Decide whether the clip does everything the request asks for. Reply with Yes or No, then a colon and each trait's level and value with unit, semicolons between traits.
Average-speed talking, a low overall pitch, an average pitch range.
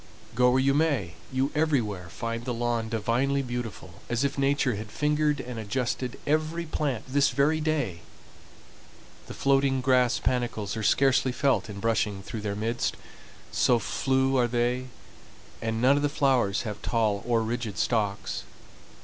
Yes: average, 155 wpm; low, 125 Hz; average, 3.6 semitones